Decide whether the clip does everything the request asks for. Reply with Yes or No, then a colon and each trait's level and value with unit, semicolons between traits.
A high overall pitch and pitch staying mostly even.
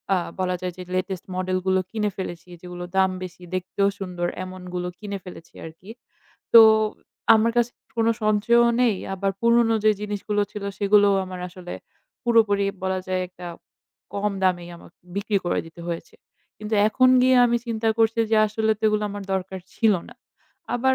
No: high, 200 Hz; average, 3.2 semitones